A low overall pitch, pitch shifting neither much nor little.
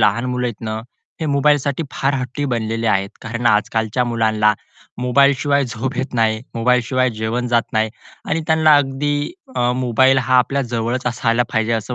Yes: low, 125 Hz; average, 3.0 semitones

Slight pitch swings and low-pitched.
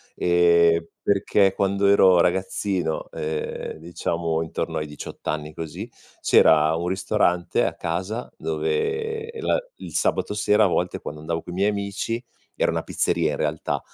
No: average, 3.7 semitones; very low, 90 Hz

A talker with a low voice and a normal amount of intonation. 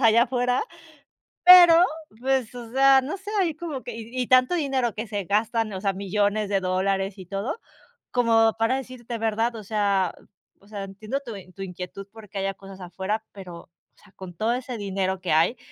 No: high, 215 Hz; average, 4.2 semitones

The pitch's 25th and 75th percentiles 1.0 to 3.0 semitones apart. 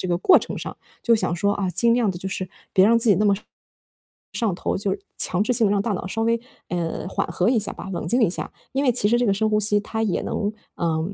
No: average, 3.5 semitones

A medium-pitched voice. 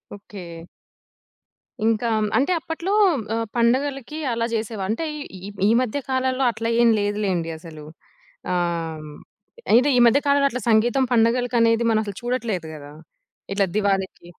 No: high, 225 Hz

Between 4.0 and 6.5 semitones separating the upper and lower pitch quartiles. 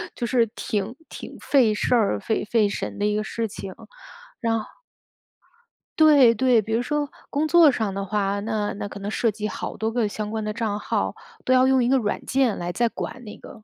No: average, 3.1 semitones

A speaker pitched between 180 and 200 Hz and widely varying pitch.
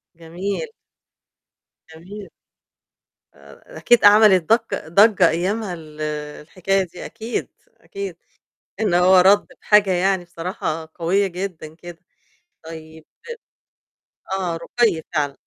No: medium, 185 Hz; average, 3.7 semitones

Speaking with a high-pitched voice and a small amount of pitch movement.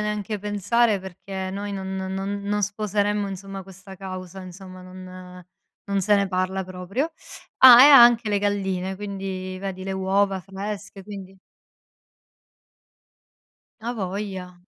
Yes: high, 195 Hz; narrow, 1.6 semitones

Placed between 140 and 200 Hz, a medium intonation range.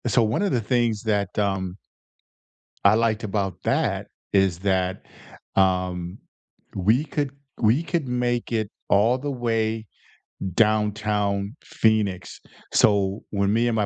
No: low, 105 Hz; average, 3.0 semitones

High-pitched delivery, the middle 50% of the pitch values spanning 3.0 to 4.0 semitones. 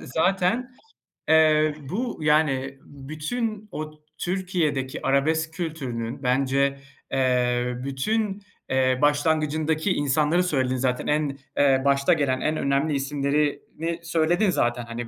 No: medium, 150 Hz; average, 3.3 semitones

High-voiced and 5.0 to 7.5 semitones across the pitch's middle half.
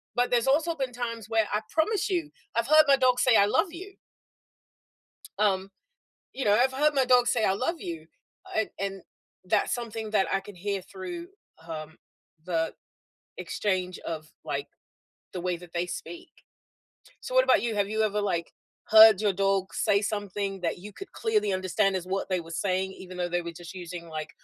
Yes: high, 205 Hz; average, 5.3 semitones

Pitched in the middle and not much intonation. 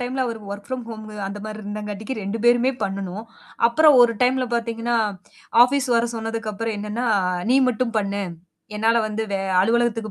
No: high, 230 Hz; narrow, 2.3 semitones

